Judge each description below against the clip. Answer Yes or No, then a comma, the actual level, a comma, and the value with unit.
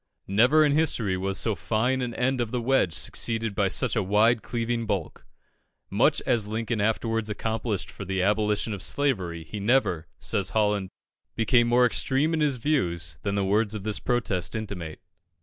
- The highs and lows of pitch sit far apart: No, average, 3.6 semitones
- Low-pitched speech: Yes, low, 110 Hz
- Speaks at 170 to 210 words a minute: Yes, average, 175 wpm